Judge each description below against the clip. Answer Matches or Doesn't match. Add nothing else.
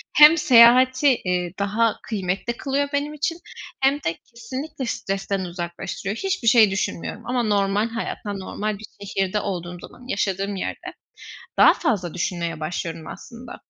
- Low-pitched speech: Doesn't match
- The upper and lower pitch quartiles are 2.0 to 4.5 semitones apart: Doesn't match